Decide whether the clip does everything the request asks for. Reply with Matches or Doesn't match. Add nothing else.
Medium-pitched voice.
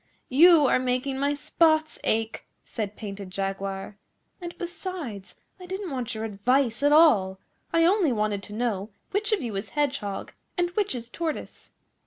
Doesn't match